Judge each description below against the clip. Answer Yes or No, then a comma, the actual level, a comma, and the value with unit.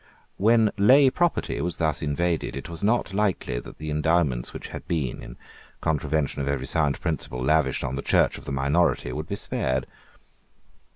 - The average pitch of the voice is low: Yes, very low, 80 Hz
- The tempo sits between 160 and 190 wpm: Yes, average, 175 wpm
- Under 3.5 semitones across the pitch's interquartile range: No, average, 4.3 semitones